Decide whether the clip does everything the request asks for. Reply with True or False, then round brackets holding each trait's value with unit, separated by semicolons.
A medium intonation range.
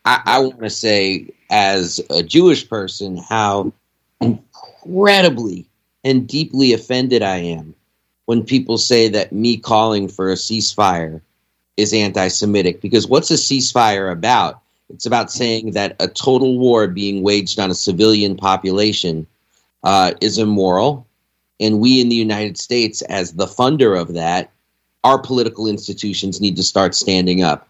True (3.7 semitones)